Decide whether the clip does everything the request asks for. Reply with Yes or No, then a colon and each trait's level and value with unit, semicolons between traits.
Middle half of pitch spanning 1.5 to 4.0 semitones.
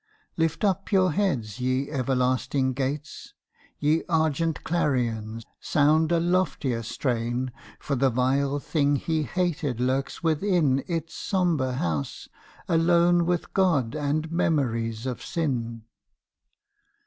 No: average, 4.6 semitones